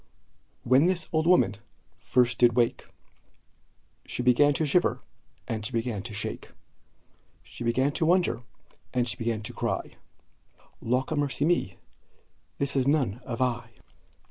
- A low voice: Yes, low, 125 Hz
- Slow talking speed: Yes, slow, 130 wpm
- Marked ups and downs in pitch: No, average, 3.7 semitones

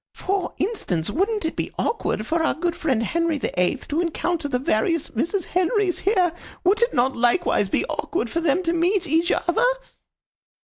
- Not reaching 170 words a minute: No, average, 180 wpm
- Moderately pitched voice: No, very high, 335 Hz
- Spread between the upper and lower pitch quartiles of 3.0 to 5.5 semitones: Yes, average, 5.2 semitones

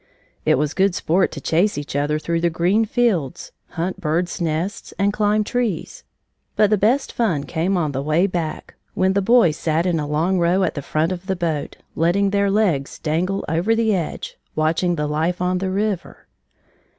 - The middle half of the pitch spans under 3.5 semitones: No, average, 3.9 semitones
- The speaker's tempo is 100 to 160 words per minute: No, average, 190 wpm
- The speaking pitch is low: No, medium, 175 Hz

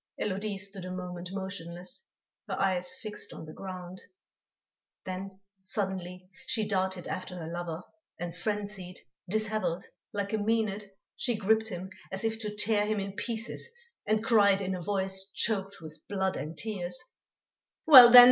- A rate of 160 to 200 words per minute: No, average, 150 wpm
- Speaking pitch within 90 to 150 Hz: No, high, 195 Hz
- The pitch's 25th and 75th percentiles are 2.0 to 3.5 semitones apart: Yes, average, 2.8 semitones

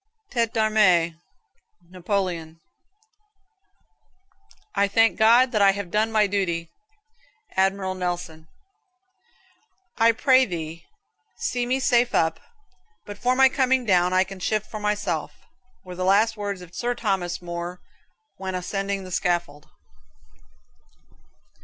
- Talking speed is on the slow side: Yes, slow, 120 wpm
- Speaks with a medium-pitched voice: No, high, 195 Hz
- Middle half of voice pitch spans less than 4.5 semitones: Yes, average, 3.9 semitones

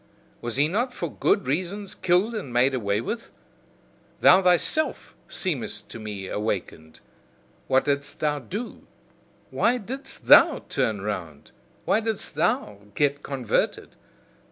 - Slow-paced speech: Yes, slow, 130 wpm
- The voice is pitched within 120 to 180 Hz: Yes, medium, 140 Hz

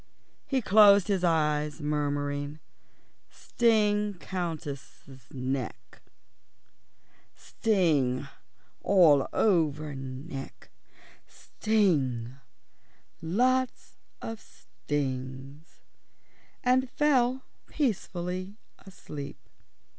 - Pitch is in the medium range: Yes, medium, 165 Hz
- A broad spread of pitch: Yes, wide, 6.5 semitones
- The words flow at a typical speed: No, slow, 55 wpm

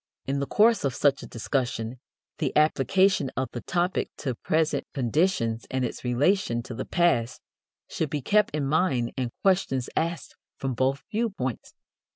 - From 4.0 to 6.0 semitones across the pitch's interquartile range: Yes, wide, 5.5 semitones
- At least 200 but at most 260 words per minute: No, average, 160 wpm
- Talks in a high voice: No, medium, 140 Hz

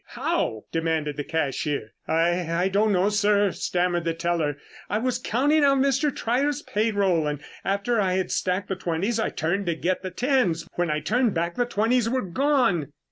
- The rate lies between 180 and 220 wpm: Yes, average, 185 wpm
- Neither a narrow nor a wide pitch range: No, wide, 5.8 semitones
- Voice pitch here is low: No, high, 190 Hz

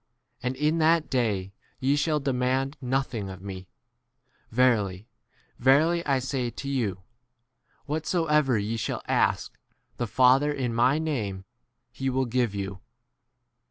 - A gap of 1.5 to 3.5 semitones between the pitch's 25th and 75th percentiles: No, average, 4.5 semitones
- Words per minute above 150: No, average, 140 wpm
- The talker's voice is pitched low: Yes, low, 130 Hz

